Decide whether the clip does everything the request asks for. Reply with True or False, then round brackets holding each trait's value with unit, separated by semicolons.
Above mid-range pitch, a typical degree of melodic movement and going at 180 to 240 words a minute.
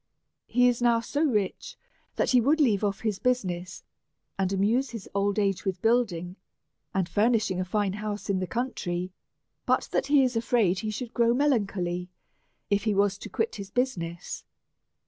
True (210 Hz; 4.2 semitones; 185 wpm)